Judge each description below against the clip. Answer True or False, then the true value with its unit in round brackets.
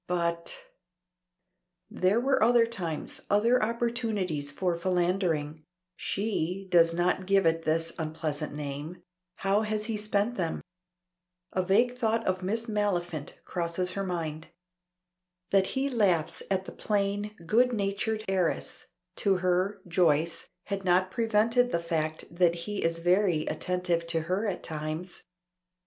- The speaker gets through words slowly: True (130 wpm)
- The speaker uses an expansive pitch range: False (3.9 semitones)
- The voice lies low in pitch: False (185 Hz)